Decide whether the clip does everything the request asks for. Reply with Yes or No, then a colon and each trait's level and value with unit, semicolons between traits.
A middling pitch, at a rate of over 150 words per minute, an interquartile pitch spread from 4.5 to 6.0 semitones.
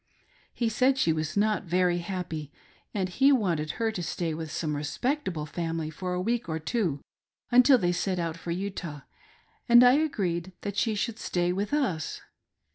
Yes: medium, 180 Hz; average, 180 wpm; wide, 5.5 semitones